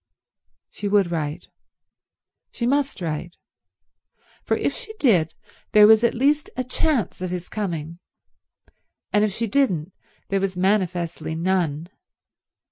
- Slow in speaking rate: Yes, slow, 125 wpm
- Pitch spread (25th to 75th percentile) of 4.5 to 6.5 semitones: Yes, average, 5.2 semitones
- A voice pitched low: No, high, 190 Hz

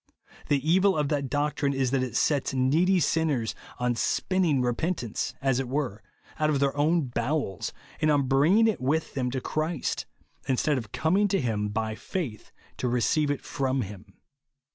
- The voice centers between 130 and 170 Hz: Yes, medium, 140 Hz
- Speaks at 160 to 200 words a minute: Yes, average, 170 wpm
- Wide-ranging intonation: No, average, 3.9 semitones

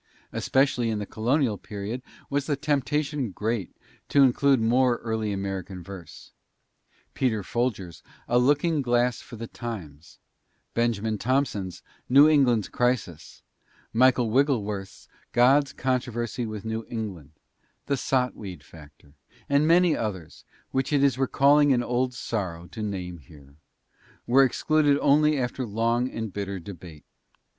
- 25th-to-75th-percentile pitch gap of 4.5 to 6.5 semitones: Yes, average, 5.0 semitones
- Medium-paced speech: No, slow, 130 wpm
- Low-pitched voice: Yes, low, 120 Hz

